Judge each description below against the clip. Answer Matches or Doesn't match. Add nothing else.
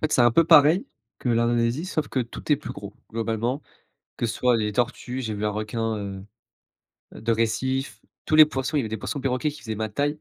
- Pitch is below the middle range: Matches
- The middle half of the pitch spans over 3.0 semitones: Matches